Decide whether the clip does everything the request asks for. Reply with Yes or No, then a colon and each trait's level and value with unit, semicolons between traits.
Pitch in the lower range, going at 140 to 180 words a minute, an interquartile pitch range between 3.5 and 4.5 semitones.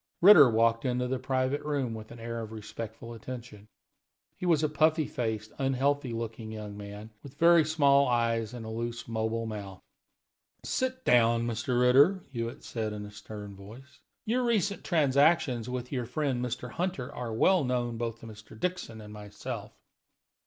Yes: low, 120 Hz; average, 165 wpm; average, 4.1 semitones